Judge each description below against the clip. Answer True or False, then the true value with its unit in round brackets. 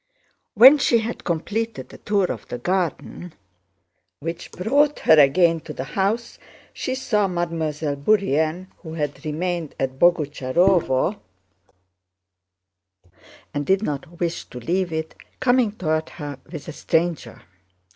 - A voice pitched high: False (170 Hz)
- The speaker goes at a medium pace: False (120 wpm)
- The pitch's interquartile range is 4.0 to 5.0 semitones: True (4.6 semitones)